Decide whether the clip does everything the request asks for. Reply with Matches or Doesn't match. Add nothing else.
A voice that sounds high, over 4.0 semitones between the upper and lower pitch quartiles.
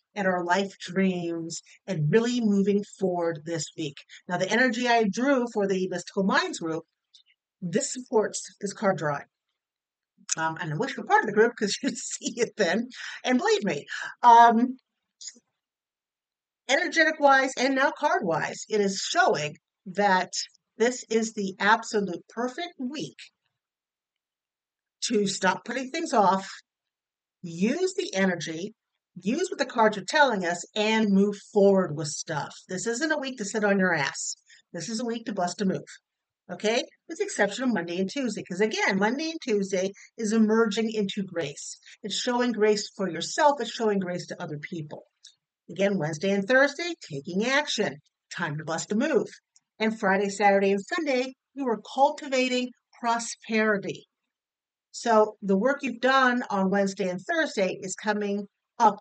Matches